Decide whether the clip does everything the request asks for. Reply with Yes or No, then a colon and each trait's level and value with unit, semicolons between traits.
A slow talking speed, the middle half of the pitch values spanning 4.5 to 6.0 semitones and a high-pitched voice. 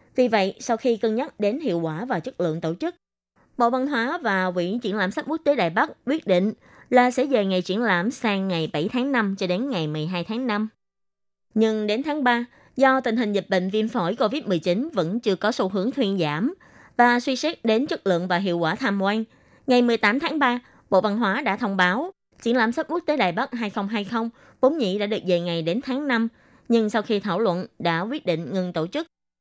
No: average, 230 wpm; average, 4.9 semitones; high, 220 Hz